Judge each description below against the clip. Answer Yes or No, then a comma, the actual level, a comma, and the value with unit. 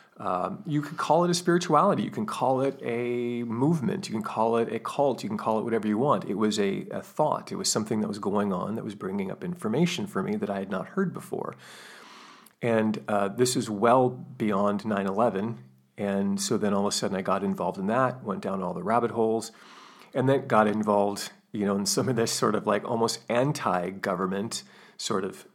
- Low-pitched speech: Yes, low, 115 Hz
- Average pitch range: No, wide, 7.3 semitones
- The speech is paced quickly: Yes, fast, 220 wpm